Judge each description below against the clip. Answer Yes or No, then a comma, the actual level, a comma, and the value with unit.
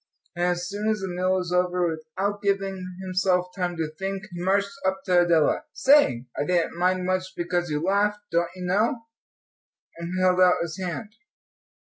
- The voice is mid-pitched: Yes, medium, 180 Hz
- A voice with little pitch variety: Yes, narrow, 1.8 semitones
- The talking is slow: No, average, 175 wpm